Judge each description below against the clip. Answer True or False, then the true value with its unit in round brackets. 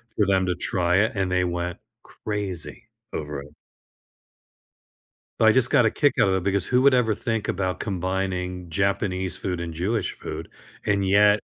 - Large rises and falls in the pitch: False (2.6 semitones)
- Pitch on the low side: True (95 Hz)